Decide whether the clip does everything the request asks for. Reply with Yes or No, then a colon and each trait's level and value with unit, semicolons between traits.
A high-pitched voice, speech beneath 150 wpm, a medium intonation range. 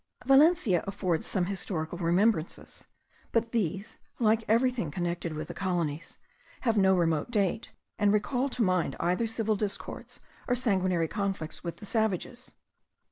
Yes: high, 195 Hz; slow, 135 wpm; average, 4.6 semitones